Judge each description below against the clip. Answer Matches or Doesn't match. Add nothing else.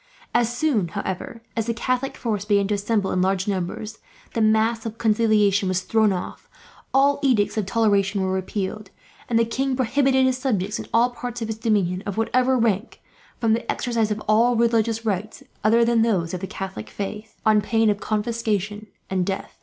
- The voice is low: Doesn't match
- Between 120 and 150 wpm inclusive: Doesn't match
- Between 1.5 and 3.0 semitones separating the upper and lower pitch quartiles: Matches